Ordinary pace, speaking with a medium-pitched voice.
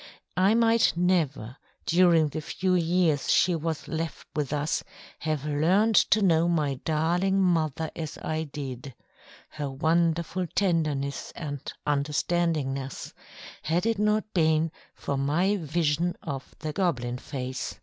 No: slow, 130 wpm; medium, 160 Hz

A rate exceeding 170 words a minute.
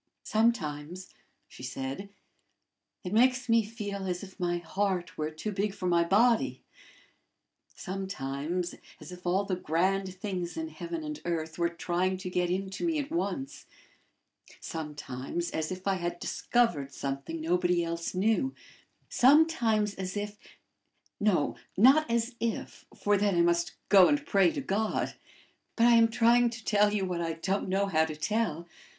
No: average, 155 wpm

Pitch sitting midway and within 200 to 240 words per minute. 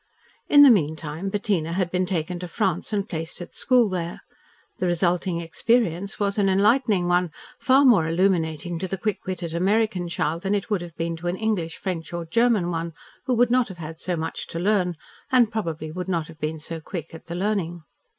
Yes: medium, 180 Hz; fast, 205 wpm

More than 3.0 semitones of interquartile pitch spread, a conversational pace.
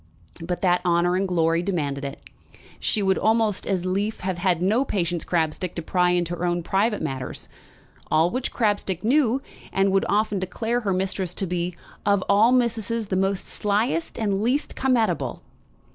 Yes: average, 3.6 semitones; average, 175 wpm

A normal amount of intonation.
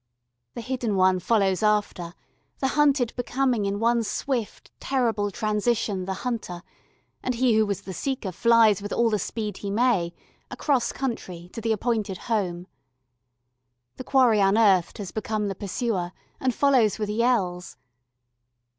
Yes: average, 3.7 semitones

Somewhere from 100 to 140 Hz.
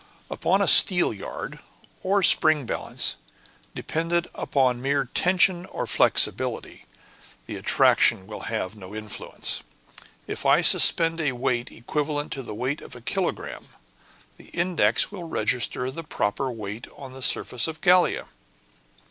Yes: low, 135 Hz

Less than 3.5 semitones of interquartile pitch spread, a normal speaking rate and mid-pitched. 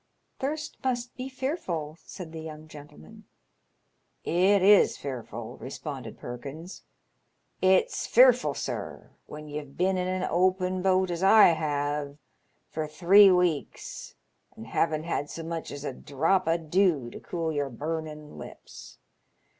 No: average, 4.0 semitones; average, 145 wpm; medium, 165 Hz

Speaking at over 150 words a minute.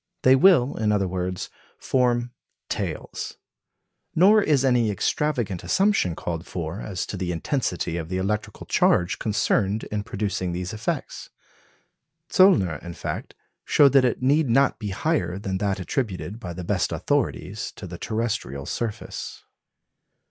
No: average, 140 wpm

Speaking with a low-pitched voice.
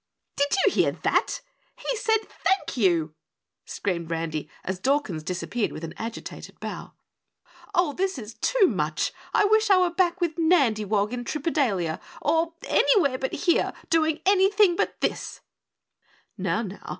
No: very high, 285 Hz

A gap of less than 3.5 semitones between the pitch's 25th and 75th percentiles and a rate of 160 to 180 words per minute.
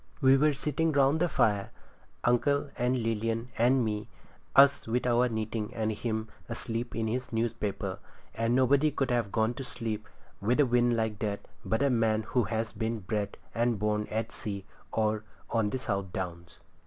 Yes: narrow, 2.5 semitones; average, 175 wpm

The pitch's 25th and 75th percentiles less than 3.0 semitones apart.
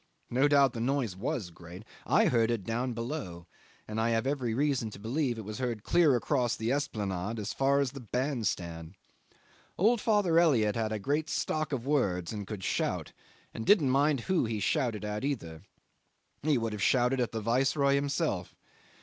No: average, 4.7 semitones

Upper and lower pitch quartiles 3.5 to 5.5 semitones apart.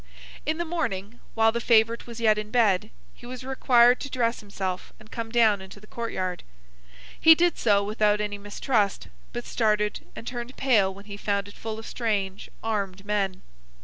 No: average, 2.8 semitones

